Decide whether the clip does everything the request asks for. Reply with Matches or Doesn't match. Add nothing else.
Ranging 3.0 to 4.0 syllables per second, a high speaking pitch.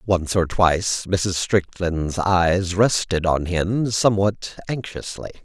Doesn't match